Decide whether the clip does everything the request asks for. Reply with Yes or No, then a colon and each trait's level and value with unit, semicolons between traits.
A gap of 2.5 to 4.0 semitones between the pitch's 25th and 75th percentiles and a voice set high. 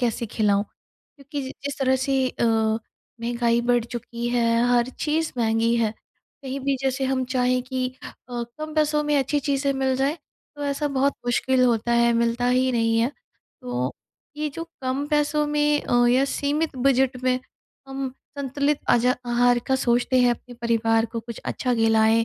Yes: average, 2.8 semitones; very high, 255 Hz